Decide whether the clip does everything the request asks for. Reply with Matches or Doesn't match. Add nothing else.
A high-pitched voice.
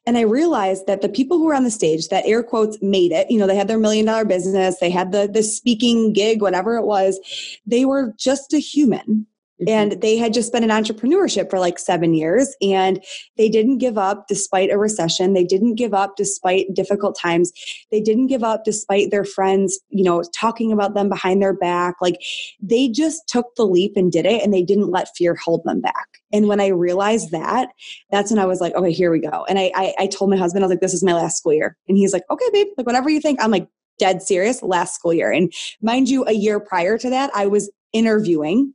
Matches